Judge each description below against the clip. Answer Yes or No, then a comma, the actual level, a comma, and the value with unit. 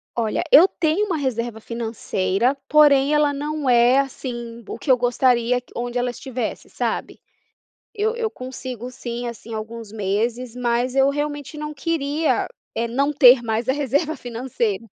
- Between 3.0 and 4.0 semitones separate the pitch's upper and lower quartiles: Yes, average, 3.5 semitones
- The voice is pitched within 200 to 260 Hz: Yes, very high, 250 Hz